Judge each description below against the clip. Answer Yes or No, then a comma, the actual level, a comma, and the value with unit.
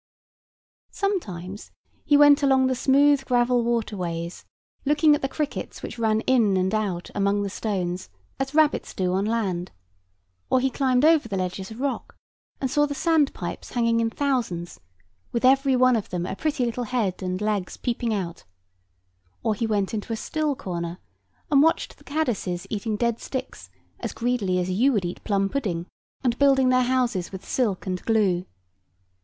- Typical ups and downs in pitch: No, wide, 5.8 semitones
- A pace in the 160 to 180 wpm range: Yes, average, 175 wpm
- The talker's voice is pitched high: Yes, high, 230 Hz